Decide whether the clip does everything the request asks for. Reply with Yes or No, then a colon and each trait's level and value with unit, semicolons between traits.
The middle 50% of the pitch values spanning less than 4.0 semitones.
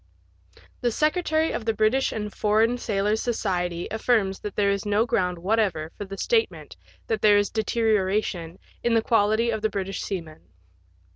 Yes: narrow, 2.6 semitones